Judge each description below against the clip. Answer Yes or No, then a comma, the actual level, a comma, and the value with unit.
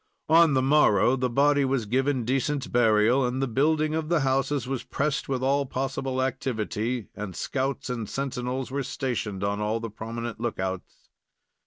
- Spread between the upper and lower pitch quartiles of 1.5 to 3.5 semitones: Yes, average, 3.0 semitones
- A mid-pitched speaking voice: No, low, 130 Hz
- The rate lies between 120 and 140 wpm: No, average, 165 wpm